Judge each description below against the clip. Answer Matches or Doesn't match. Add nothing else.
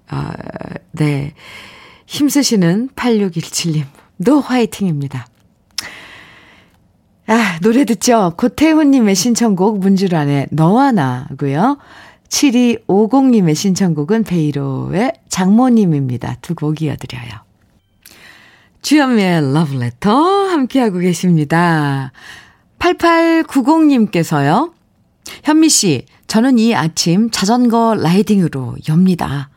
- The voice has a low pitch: Doesn't match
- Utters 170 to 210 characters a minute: Matches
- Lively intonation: Matches